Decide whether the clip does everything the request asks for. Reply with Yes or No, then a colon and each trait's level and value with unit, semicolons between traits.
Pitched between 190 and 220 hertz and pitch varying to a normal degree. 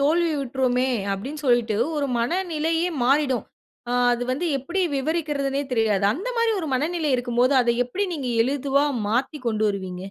No: very high, 275 Hz; average, 4.4 semitones